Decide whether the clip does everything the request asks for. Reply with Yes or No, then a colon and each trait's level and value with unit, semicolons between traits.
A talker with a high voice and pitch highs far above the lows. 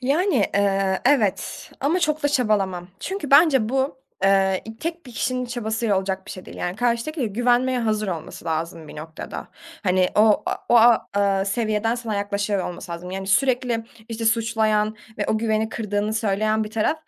No: high, 220 Hz; average, 3.8 semitones